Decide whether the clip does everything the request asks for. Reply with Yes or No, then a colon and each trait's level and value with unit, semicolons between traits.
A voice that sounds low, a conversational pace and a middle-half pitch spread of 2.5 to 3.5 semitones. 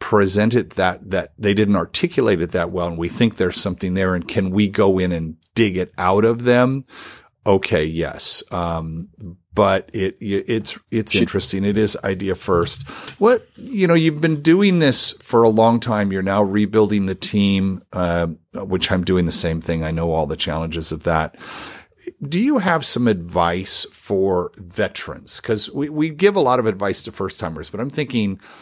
No: low, 100 Hz; average, 185 wpm; average, 4.6 semitones